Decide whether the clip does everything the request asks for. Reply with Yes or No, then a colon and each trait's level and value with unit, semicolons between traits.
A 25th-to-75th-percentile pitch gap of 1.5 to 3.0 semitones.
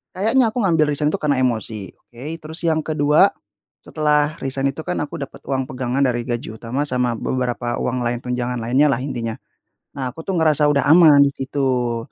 No: average, 3.7 semitones